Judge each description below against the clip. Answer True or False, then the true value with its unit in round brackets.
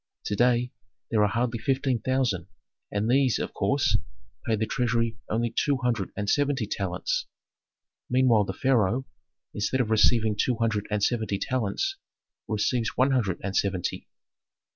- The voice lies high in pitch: False (115 Hz)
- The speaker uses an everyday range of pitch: True (3.5 semitones)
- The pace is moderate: True (145 wpm)